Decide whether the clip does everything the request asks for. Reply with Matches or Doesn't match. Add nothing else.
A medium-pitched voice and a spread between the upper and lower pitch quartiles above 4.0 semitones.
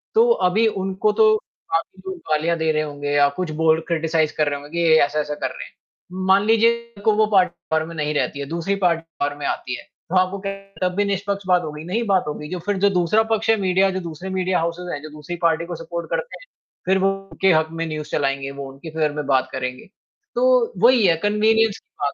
Matches